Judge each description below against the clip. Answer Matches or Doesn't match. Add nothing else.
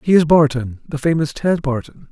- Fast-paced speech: Doesn't match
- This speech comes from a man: Matches